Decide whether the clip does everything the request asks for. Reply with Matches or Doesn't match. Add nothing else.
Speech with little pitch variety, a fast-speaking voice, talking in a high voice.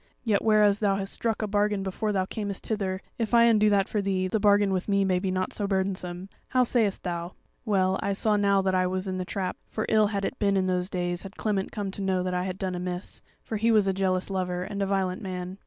Matches